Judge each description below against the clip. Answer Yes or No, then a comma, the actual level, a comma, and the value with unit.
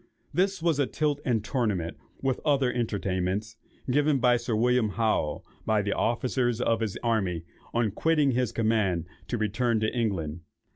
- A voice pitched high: No, low, 115 Hz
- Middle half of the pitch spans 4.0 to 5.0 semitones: No, average, 3.5 semitones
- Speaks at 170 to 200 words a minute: No, average, 155 wpm